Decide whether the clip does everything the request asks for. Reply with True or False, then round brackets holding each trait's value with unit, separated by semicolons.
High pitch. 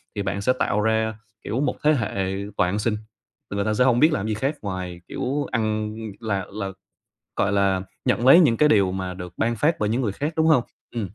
False (110 Hz)